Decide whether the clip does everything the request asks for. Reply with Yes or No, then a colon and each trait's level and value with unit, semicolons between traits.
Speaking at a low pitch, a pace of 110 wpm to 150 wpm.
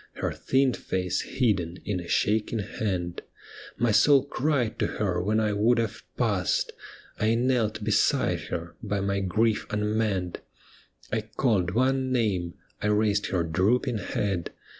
Yes: low, 105 Hz; average, 140 wpm